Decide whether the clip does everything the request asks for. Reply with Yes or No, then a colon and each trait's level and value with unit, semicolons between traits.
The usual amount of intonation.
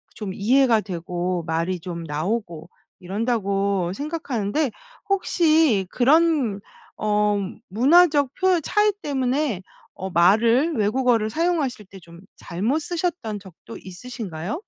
No: wide, 7.6 semitones